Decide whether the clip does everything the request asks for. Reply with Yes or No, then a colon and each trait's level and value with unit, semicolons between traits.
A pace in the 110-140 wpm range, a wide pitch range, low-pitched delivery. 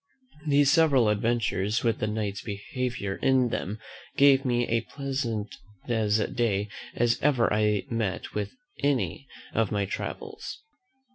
No: slow, 135 wpm; average, 4.0 semitones; low, 115 Hz